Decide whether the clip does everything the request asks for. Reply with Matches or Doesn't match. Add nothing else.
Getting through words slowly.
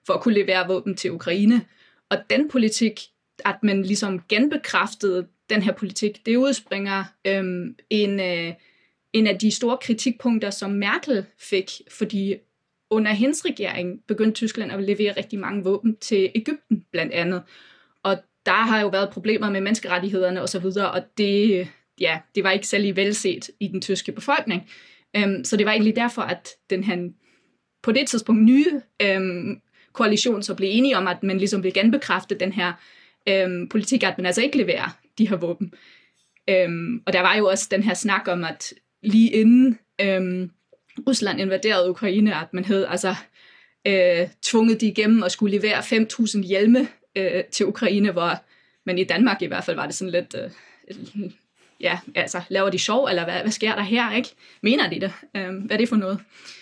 Doesn't match